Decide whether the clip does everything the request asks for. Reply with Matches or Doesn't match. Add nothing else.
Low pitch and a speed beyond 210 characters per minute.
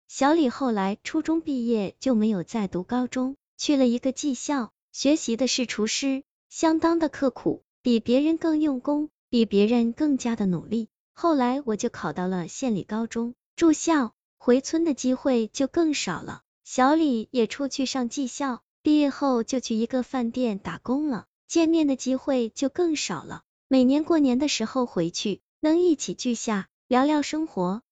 Doesn't match